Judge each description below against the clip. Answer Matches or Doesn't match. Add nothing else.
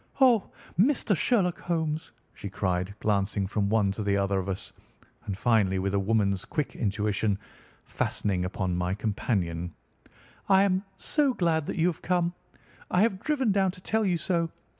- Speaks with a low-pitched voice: Matches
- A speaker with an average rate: Matches